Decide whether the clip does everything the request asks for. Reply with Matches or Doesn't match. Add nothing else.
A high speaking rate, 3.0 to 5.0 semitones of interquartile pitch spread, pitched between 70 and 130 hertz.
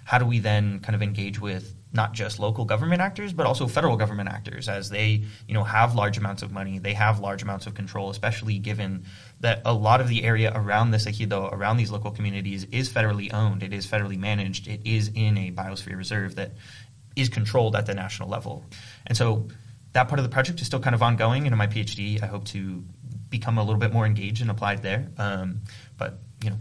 Doesn't match